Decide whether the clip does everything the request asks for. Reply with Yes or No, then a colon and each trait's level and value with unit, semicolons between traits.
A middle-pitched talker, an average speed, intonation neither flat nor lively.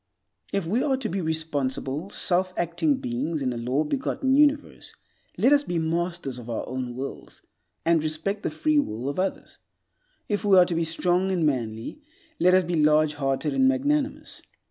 No: medium, 170 Hz; average, 180 wpm; wide, 6.2 semitones